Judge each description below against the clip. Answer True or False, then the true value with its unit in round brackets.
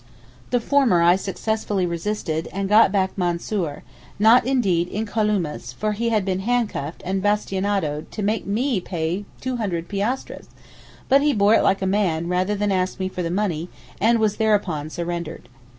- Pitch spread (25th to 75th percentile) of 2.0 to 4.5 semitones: True (3.7 semitones)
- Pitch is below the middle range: False (195 Hz)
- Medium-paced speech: True (165 wpm)